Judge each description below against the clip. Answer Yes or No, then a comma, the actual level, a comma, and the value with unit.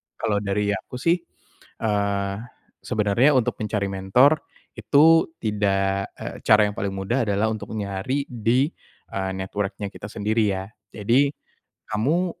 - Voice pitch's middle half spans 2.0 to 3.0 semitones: No, average, 3.8 semitones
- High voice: No, low, 105 Hz